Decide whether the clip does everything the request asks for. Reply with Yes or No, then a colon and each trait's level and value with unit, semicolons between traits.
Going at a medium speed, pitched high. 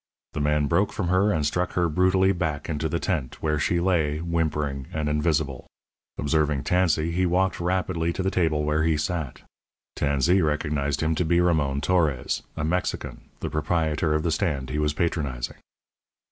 No: average, 175 wpm; very low, 80 Hz